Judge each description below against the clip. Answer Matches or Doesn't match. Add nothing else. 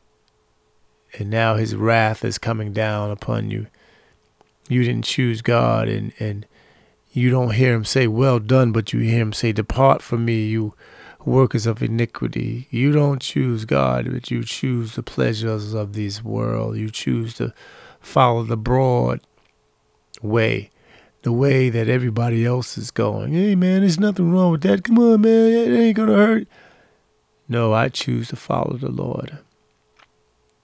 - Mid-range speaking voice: Doesn't match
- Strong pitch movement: Doesn't match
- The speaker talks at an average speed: Matches